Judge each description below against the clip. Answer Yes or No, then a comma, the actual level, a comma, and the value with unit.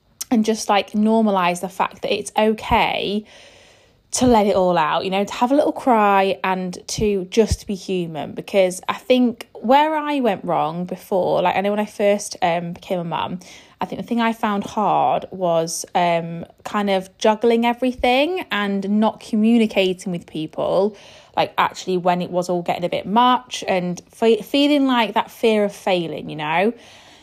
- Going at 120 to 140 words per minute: No, average, 180 wpm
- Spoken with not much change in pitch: No, average, 3.7 semitones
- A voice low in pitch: No, high, 205 Hz